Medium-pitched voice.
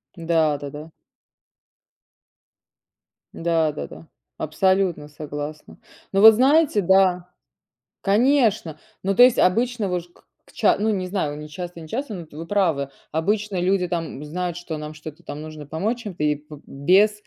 Yes: medium, 175 Hz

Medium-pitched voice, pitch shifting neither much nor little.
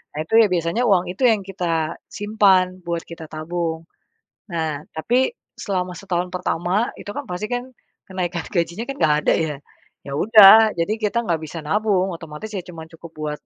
Yes: medium, 180 Hz; average, 4.0 semitones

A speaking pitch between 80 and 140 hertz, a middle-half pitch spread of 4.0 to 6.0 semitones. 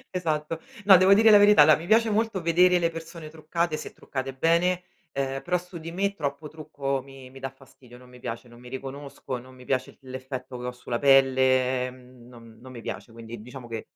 Yes: low, 135 Hz; average, 4.8 semitones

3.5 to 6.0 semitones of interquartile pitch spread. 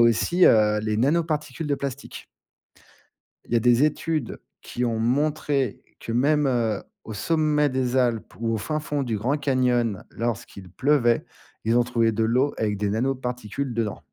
Yes: average, 4.1 semitones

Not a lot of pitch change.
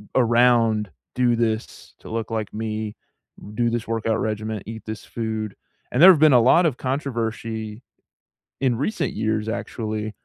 Yes: narrow, 1.8 semitones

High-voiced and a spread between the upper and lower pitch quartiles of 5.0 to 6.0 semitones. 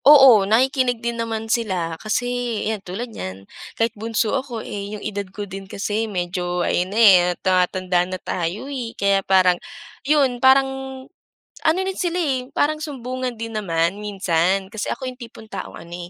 Yes: high, 215 Hz; wide, 5.4 semitones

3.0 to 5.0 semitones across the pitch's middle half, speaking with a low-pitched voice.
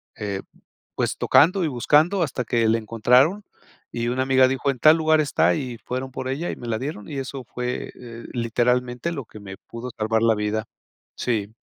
Yes: average, 3.3 semitones; low, 125 Hz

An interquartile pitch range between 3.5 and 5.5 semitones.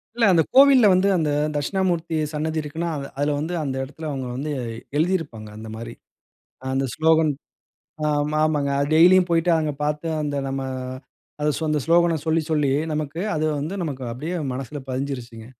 No: average, 2.8 semitones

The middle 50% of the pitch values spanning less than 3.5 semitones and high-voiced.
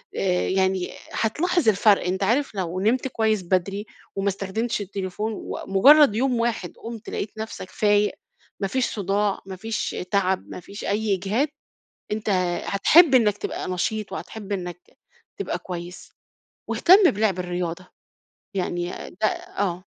Yes: average, 2.9 semitones; high, 200 Hz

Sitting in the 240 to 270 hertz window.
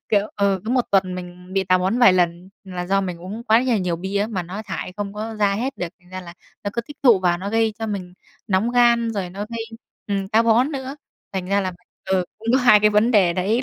No: high, 200 Hz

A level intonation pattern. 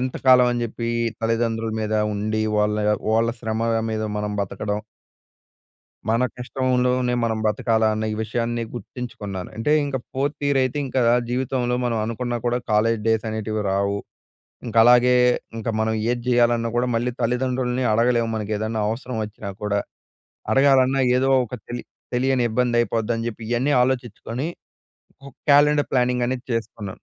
Yes: narrow, 2.3 semitones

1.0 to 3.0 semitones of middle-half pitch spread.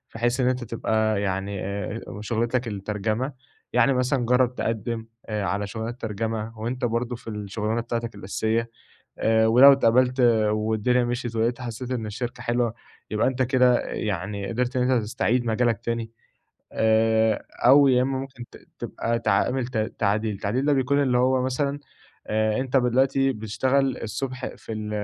Yes: narrow, 2.6 semitones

